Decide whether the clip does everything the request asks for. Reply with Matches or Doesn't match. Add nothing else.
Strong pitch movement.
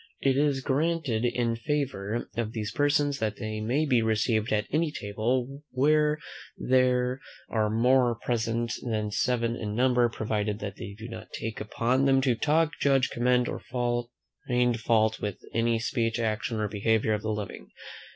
Doesn't match